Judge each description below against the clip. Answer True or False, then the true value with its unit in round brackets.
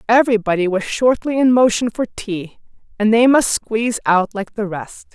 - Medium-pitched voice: False (220 Hz)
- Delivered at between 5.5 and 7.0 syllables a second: False (4.9 syllables/s)